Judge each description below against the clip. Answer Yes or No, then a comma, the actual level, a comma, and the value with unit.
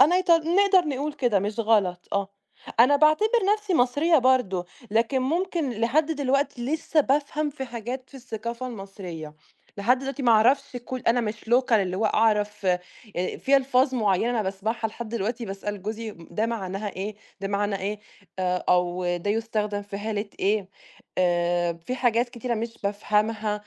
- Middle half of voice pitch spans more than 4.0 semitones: Yes, average, 4.5 semitones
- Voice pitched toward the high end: Yes, high, 225 Hz